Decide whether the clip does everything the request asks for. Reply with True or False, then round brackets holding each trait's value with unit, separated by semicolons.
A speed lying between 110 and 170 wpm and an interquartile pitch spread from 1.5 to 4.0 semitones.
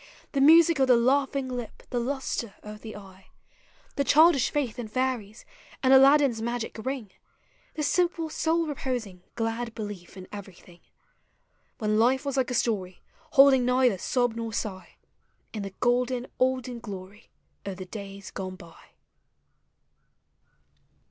False (140 wpm; 4.4 semitones)